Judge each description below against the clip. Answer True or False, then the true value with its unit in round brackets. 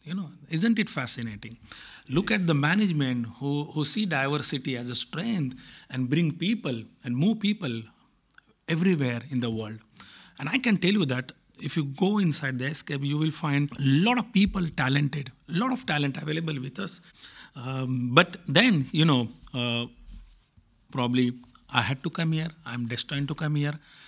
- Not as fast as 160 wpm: False (175 wpm)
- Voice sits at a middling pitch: True (145 Hz)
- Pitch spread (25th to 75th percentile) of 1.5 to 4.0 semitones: False (5.3 semitones)